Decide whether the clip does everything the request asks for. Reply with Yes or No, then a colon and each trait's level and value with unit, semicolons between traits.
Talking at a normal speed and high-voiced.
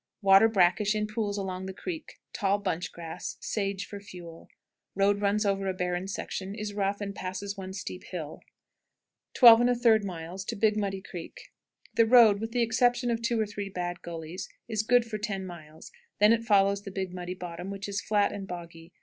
Yes: average, 185 wpm; high, 200 Hz